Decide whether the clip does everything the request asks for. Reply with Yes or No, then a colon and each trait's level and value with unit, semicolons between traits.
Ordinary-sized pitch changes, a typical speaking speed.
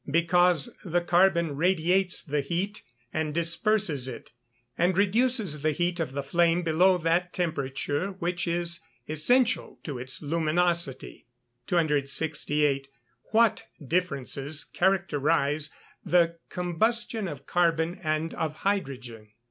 No: average, 3.4 semitones; slow, 115 wpm